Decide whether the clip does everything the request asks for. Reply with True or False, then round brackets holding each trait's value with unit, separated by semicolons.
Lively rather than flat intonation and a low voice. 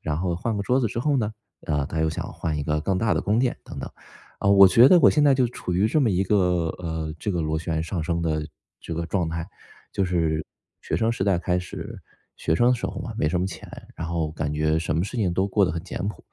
False (4.7 semitones; 90 Hz)